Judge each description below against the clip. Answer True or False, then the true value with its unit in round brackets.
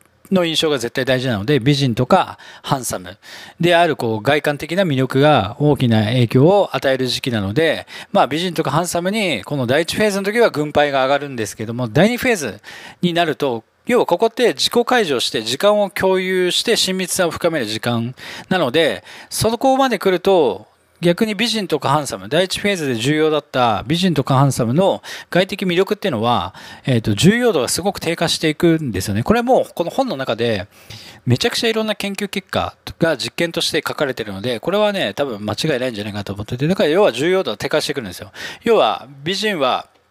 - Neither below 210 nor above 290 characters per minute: False (405 characters per minute)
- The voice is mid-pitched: True (155 Hz)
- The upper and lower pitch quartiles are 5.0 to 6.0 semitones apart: False (7.0 semitones)